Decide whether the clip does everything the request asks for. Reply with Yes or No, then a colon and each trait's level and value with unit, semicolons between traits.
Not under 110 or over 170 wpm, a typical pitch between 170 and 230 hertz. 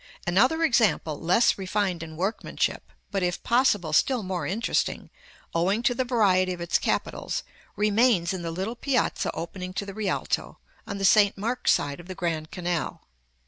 Yes: average, 165 wpm; high, 190 Hz